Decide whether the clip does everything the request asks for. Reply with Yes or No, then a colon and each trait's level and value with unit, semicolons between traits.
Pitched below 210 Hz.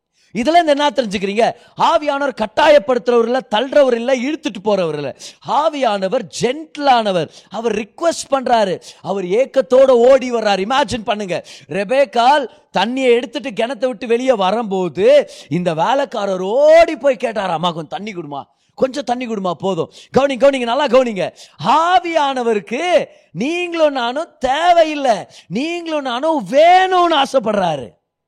No: very high, 255 Hz